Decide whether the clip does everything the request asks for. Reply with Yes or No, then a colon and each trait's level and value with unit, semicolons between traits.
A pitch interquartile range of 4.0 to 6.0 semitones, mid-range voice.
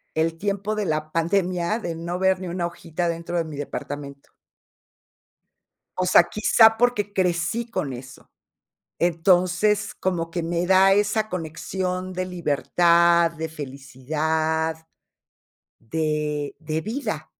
No: average, 2.9 semitones; medium, 170 Hz